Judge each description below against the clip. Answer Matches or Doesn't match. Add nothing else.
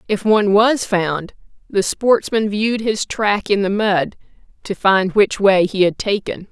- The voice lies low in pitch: Doesn't match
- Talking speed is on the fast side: Doesn't match